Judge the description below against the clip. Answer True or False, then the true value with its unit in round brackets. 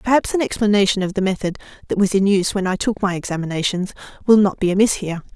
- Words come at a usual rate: False (225 wpm)